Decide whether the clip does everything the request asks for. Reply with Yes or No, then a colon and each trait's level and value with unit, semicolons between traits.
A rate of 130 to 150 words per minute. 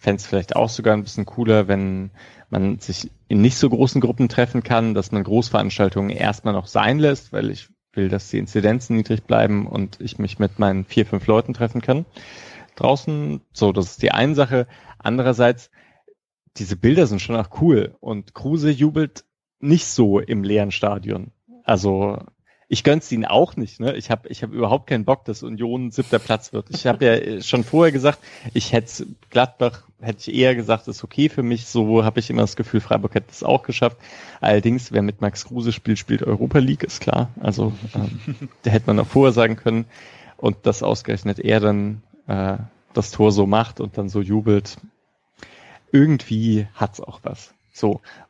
No: fast, 190 wpm